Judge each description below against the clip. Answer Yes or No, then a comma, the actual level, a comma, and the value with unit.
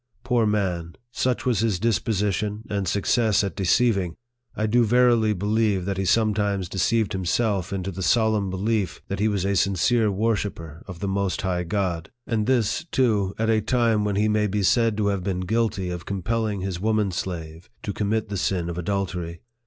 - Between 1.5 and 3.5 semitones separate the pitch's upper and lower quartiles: Yes, average, 2.8 semitones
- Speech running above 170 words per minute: Yes, average, 185 wpm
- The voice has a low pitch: Yes, low, 100 Hz